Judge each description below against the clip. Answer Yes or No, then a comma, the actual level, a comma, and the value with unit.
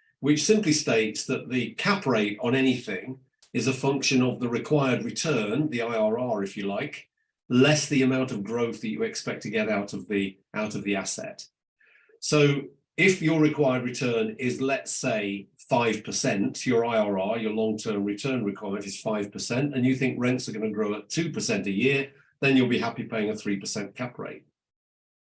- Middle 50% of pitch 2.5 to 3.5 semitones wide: No, average, 5.0 semitones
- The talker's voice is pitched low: Yes, low, 125 Hz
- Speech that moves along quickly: No, average, 180 wpm